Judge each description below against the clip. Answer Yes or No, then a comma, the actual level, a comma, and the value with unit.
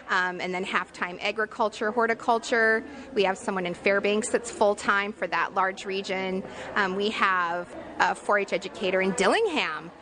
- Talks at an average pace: Yes, average, 170 wpm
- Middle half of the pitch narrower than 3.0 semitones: Yes, narrow, 2.5 semitones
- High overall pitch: Yes, high, 200 Hz